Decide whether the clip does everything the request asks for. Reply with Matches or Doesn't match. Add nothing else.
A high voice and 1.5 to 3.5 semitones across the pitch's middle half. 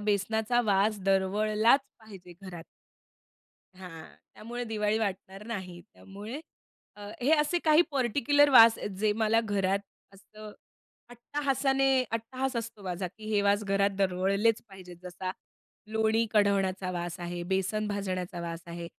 Matches